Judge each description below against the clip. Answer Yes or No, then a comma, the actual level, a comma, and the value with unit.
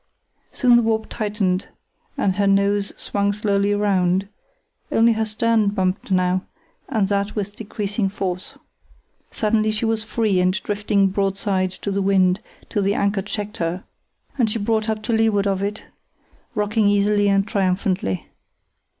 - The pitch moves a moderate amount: No, narrow, 1.7 semitones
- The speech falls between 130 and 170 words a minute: Yes, average, 150 wpm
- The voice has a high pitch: Yes, high, 205 Hz